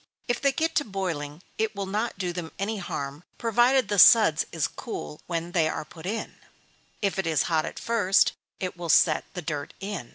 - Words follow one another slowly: No, average, 200 wpm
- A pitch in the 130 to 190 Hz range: Yes, medium, 185 Hz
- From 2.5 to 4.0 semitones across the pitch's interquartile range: No, average, 5.1 semitones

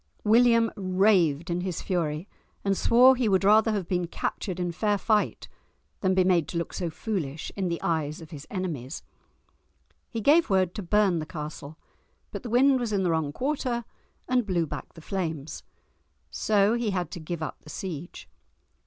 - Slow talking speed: No, average, 180 wpm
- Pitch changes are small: No, average, 4.6 semitones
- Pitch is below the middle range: No, medium, 185 Hz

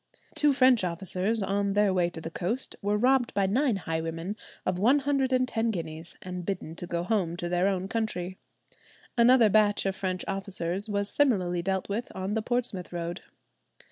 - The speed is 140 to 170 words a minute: No, average, 180 wpm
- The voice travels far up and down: No, average, 4.2 semitones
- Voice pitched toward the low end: No, high, 195 Hz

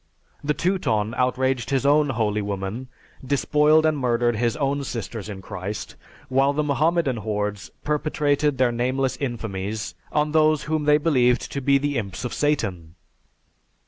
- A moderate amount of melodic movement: Yes, average, 5.0 semitones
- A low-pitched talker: Yes, low, 130 Hz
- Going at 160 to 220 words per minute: No, average, 145 wpm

